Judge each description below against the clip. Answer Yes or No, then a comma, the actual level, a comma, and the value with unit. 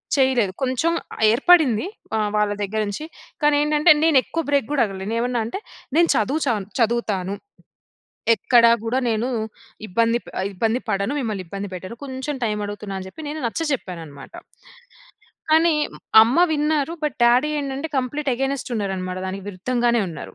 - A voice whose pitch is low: No, high, 235 Hz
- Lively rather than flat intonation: Yes, wide, 5.7 semitones